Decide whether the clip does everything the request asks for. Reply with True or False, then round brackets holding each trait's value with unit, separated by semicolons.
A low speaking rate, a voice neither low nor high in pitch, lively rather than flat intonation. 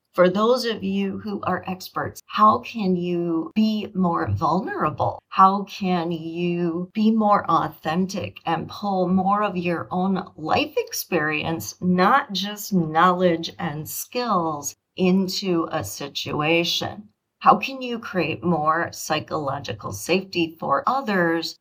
False (120 wpm; 180 Hz; 3.5 semitones)